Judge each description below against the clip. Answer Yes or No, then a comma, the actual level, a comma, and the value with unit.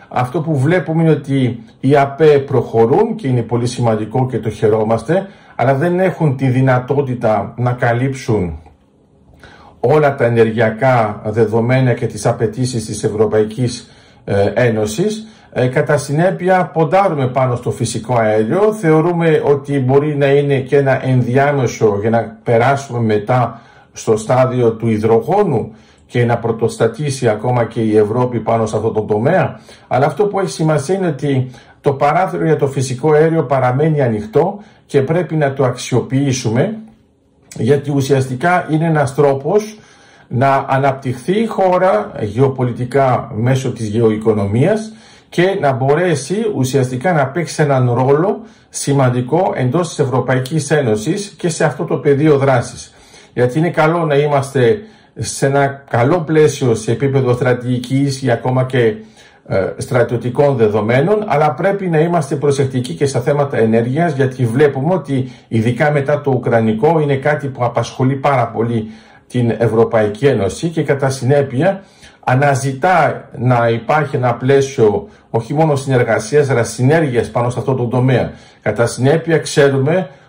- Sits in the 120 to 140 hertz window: Yes, low, 135 Hz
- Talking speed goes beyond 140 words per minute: No, average, 135 wpm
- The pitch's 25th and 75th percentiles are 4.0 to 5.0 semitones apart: Yes, average, 4.4 semitones